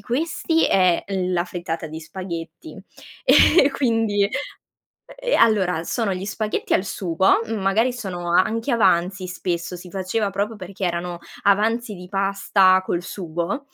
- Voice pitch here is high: Yes, high, 195 Hz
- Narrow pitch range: No, average, 3.4 semitones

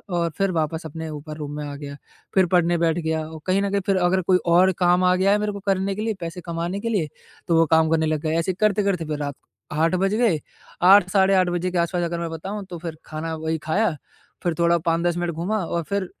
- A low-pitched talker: No, medium, 175 Hz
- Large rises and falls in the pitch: No, average, 2.9 semitones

